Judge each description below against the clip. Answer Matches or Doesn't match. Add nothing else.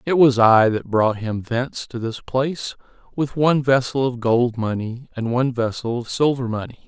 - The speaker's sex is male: Matches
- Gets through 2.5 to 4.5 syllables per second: Doesn't match